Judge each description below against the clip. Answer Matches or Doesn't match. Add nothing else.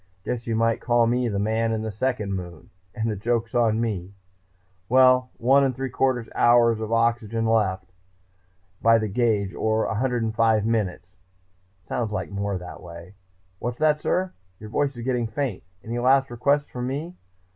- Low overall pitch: Matches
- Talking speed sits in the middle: Matches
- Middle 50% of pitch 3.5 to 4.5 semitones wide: Doesn't match